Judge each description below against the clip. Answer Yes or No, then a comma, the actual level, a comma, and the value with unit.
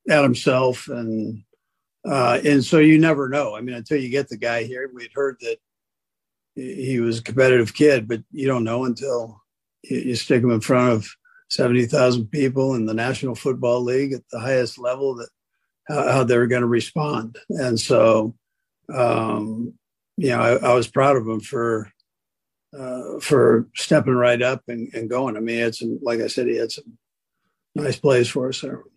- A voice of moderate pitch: No, low, 125 Hz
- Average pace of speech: Yes, average, 190 wpm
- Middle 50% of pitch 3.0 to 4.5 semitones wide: No, narrow, 2.6 semitones